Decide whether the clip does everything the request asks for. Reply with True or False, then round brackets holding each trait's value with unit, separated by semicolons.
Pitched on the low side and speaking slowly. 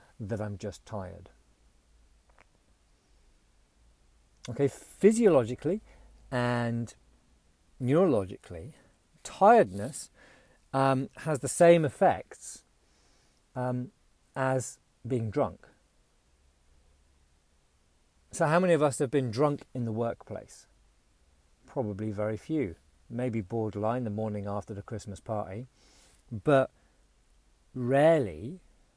True (110 Hz; 85 wpm)